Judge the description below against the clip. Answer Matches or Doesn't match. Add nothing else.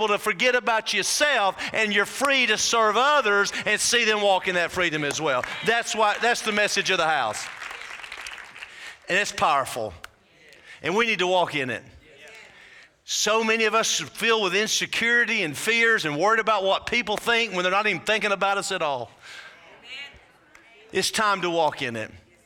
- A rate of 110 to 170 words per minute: Doesn't match